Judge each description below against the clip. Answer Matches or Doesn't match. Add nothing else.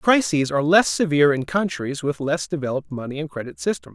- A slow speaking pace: Doesn't match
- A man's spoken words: Matches